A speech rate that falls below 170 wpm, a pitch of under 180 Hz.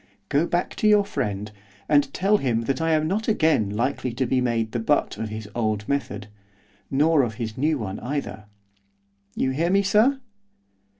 No: average, 180 wpm; low, 135 Hz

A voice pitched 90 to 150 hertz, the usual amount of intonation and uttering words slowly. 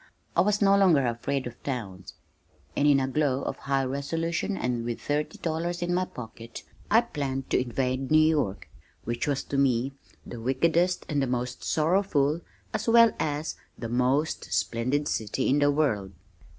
No: medium, 140 Hz; average, 4.3 semitones; average, 170 wpm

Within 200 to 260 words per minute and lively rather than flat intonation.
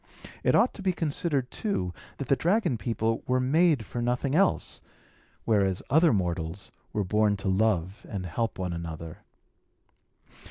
No: average, 150 wpm; wide, 7.1 semitones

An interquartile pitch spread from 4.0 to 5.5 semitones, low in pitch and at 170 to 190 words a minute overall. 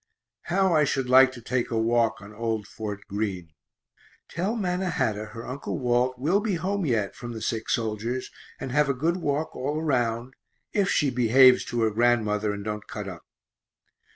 Yes: average, 5.1 semitones; low, 120 Hz; average, 180 wpm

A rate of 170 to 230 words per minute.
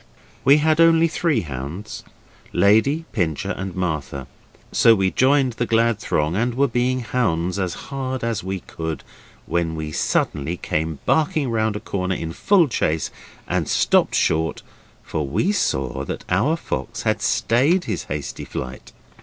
No: average, 155 wpm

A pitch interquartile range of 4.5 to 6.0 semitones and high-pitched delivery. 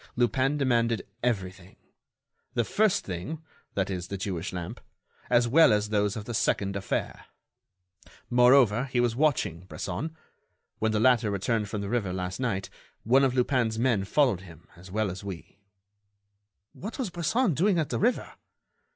No: average, 5.1 semitones; low, 115 Hz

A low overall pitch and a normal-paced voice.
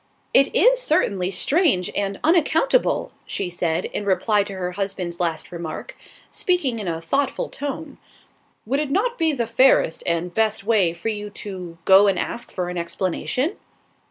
No: high, 205 Hz; average, 160 wpm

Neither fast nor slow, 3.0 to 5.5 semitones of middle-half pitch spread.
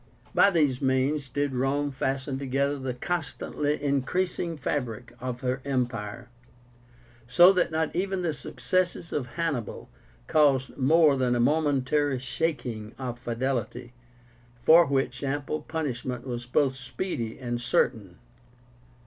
No: slow, 125 wpm; average, 3.3 semitones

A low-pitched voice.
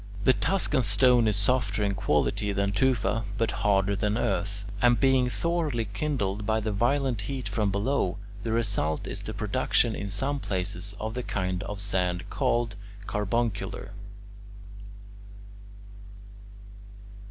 Yes: low, 105 Hz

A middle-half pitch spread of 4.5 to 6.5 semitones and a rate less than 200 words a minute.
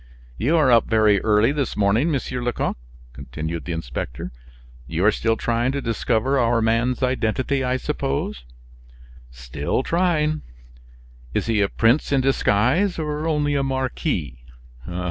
Yes: average, 5.2 semitones; average, 140 wpm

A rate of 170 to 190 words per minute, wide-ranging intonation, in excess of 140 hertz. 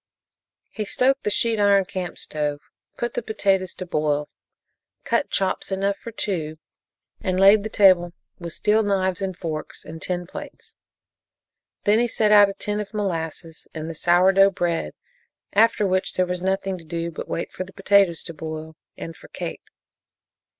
No: average, 175 wpm; average, 3.3 semitones; medium, 185 Hz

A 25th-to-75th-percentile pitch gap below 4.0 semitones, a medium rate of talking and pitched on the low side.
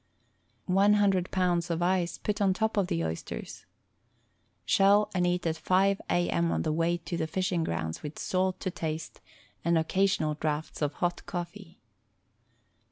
No: average, 2.9 semitones; average, 165 wpm; medium, 175 Hz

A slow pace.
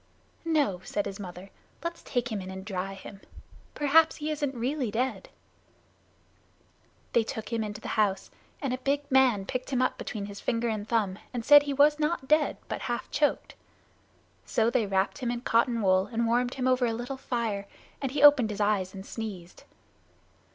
No: average, 185 wpm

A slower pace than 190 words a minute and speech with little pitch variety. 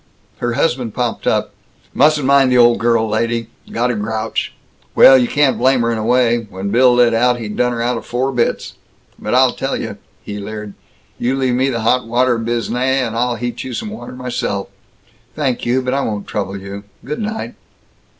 No: average, 200 wpm; narrow, 2.2 semitones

